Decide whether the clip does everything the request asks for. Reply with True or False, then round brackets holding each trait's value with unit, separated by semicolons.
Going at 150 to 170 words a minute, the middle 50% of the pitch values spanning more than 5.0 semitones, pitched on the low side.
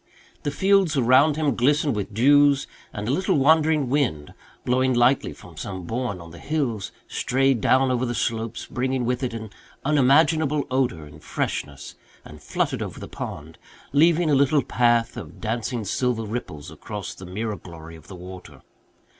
True (165 wpm; 5.5 semitones; 125 Hz)